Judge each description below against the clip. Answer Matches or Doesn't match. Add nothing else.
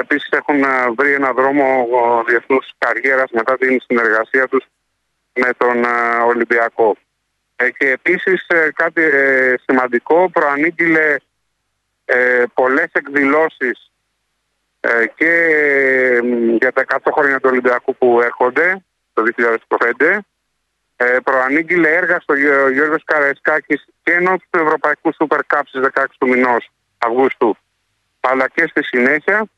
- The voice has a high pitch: Doesn't match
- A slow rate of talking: Matches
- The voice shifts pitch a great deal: Doesn't match